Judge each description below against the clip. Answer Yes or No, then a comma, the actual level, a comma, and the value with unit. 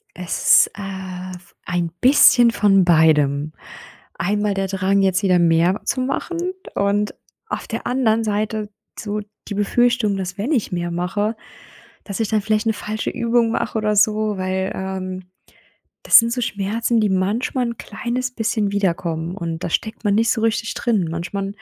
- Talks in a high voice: Yes, high, 205 Hz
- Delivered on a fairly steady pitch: No, average, 3.3 semitones